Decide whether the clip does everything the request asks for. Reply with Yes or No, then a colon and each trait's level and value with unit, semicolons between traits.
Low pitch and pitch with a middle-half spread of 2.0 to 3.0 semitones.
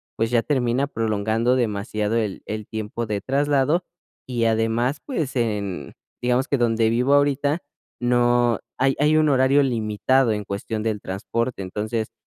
No: low, 120 Hz; average, 3.5 semitones